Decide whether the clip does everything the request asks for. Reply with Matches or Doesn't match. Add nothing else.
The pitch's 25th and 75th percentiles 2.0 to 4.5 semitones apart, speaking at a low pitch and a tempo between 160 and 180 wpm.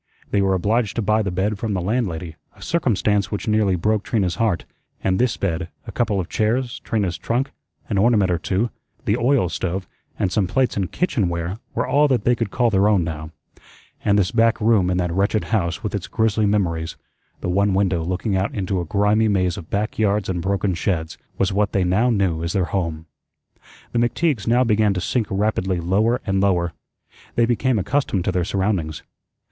Doesn't match